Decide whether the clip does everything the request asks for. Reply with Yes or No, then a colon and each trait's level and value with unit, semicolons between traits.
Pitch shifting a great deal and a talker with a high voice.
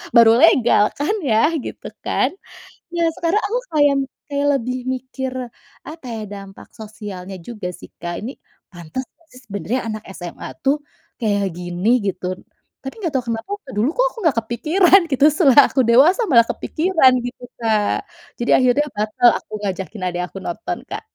Yes: wide, 5.9 semitones; high, 240 Hz